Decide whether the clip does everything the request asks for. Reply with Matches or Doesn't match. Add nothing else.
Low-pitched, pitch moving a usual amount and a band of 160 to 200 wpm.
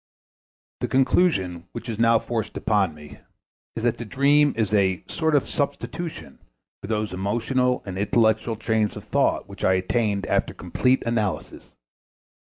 Doesn't match